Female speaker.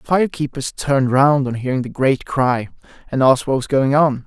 No: male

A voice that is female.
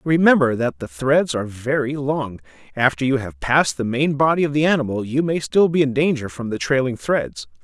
No: male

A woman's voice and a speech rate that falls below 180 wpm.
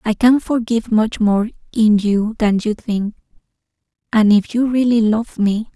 Yes: female; average, 165 wpm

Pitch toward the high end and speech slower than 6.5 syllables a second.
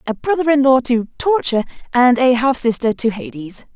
Yes: very high, 255 Hz; 5.4 syllables/s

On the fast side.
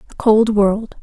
No: average, 175 wpm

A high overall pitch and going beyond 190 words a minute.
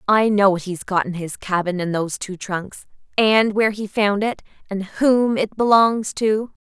Yes: high, 200 Hz; average, 200 wpm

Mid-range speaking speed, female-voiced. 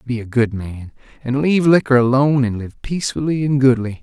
No: average, 195 wpm; male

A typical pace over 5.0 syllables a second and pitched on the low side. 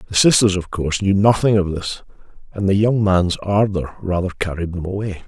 Yes: 5.4 syllables/s; very low, 95 Hz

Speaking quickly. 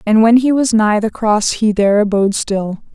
Yes: fast, 225 wpm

